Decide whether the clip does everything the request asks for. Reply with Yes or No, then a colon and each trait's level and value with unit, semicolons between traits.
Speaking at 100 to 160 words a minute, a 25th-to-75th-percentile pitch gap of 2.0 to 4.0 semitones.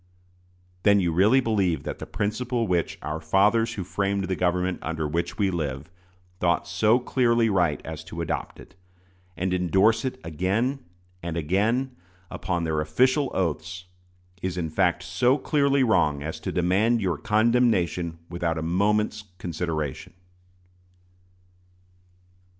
No: slow, 135 wpm; average, 4.9 semitones